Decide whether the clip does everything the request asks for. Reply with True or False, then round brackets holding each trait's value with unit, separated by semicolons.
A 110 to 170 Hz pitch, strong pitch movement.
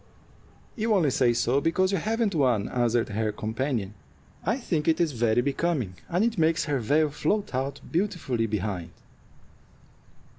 True (140 Hz; 6.8 semitones)